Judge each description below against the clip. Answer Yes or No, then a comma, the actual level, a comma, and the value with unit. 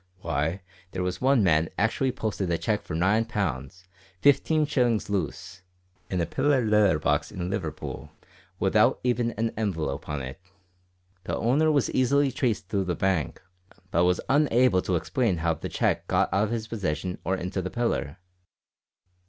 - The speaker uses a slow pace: No, average, 165 wpm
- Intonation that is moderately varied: No, wide, 5.7 semitones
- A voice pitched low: Yes, very low, 95 Hz